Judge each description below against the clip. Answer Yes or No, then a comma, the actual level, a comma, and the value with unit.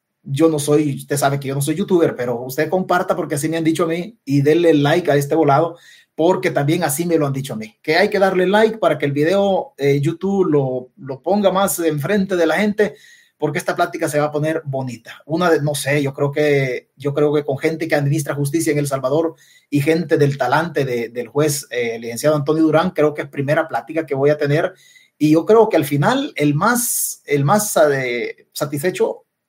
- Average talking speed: No, fast, 230 wpm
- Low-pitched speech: No, medium, 155 Hz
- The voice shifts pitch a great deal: No, average, 3.3 semitones